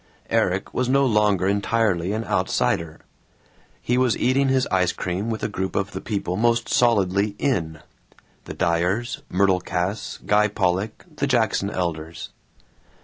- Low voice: Yes, low, 100 Hz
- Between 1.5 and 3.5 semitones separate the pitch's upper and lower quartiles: No, average, 4.1 semitones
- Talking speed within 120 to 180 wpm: Yes, average, 145 wpm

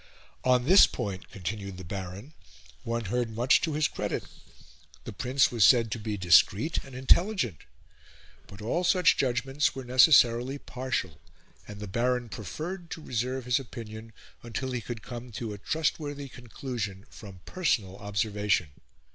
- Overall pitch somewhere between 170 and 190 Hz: No, low, 120 Hz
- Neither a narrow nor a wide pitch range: Yes, average, 4.1 semitones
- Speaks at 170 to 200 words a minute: No, average, 145 wpm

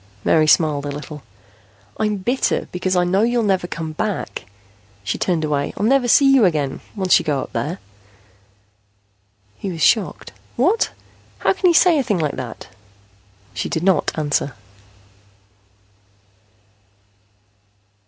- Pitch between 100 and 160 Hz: No, medium, 180 Hz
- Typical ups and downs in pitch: No, wide, 6.4 semitones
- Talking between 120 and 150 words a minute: Yes, average, 140 wpm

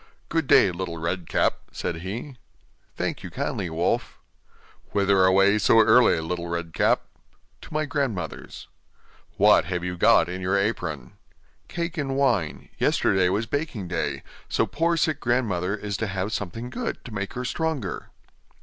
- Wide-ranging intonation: Yes, wide, 6.1 semitones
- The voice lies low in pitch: Yes, low, 100 Hz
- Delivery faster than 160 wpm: No, average, 155 wpm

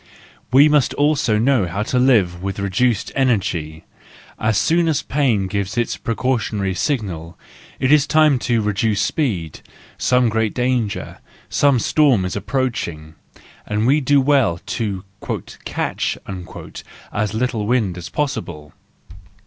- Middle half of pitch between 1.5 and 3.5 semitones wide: No, average, 5.3 semitones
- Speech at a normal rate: No, slow, 130 wpm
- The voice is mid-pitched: No, low, 115 Hz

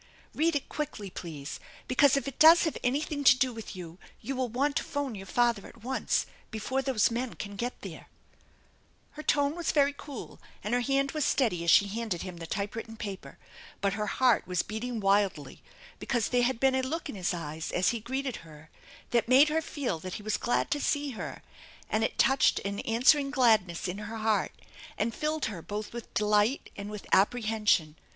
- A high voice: Yes, high, 230 Hz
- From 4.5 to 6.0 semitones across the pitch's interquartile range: Yes, average, 5.1 semitones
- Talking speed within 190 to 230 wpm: Yes, average, 200 wpm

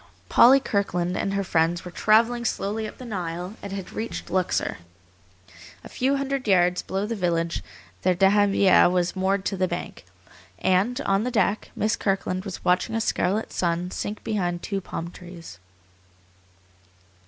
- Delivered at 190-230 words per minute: No, average, 155 wpm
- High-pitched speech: Yes, high, 195 Hz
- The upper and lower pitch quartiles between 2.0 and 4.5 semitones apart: Yes, average, 3.2 semitones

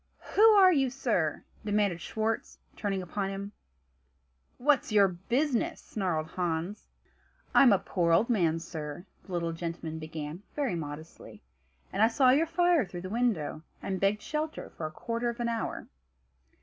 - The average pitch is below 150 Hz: No, high, 200 Hz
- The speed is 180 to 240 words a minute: No, average, 155 wpm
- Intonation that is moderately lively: No, wide, 6.3 semitones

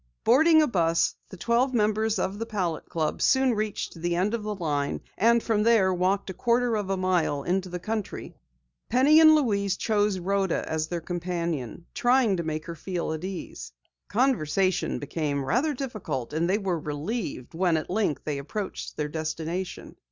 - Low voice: No, high, 190 Hz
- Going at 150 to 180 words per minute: Yes, average, 175 wpm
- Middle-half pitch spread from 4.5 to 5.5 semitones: Yes, average, 5.0 semitones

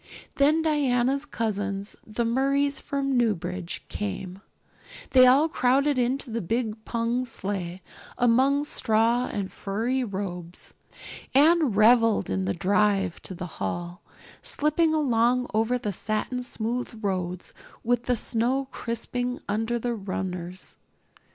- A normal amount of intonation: Yes, average, 4.4 semitones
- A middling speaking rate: No, slow, 120 wpm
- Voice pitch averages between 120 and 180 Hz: No, high, 230 Hz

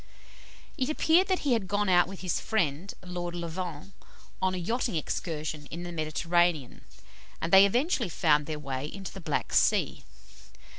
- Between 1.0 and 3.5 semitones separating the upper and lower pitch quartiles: No, average, 4.1 semitones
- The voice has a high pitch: No, medium, 175 Hz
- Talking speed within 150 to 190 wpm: Yes, average, 160 wpm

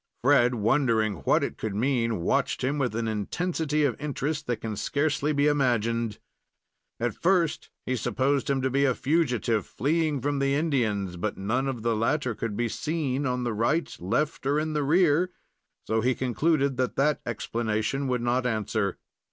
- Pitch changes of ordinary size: Yes, average, 4.2 semitones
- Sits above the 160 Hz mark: No, low, 130 Hz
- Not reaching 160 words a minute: No, average, 175 wpm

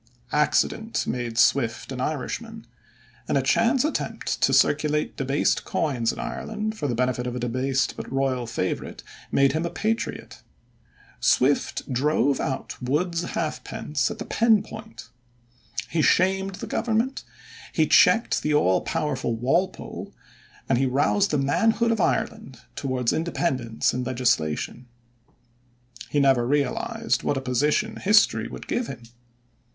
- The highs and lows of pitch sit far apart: Yes, wide, 7.3 semitones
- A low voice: No, medium, 145 Hz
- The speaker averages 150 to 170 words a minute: No, slow, 135 wpm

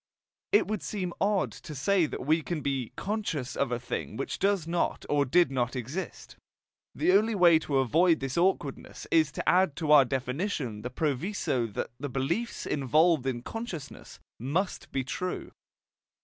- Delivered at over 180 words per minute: No, average, 165 wpm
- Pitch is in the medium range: Yes, medium, 155 Hz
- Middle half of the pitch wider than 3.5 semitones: Yes, wide, 5.5 semitones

